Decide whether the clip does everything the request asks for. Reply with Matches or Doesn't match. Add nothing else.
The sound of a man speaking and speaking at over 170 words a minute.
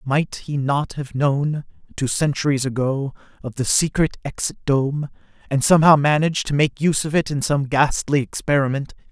Doesn't match